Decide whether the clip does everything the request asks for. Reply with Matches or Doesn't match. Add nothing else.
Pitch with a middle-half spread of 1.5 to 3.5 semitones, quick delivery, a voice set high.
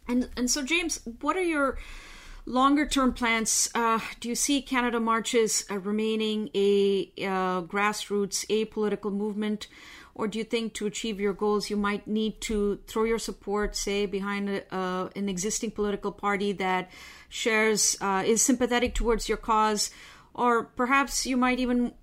Doesn't match